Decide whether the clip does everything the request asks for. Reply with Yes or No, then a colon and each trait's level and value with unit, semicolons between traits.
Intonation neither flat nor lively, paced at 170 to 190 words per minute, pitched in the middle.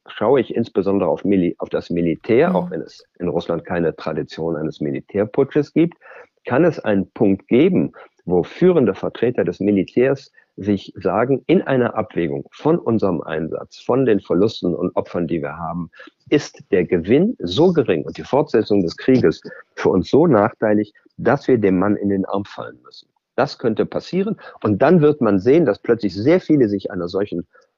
No: average, 4.6 semitones; average, 175 wpm; low, 100 Hz